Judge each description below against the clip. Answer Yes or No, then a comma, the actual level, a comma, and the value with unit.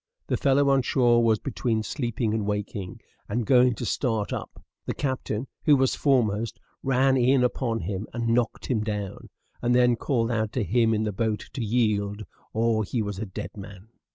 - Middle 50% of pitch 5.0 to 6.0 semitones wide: No, average, 2.9 semitones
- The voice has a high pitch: No, low, 115 Hz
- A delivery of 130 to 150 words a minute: No, average, 185 wpm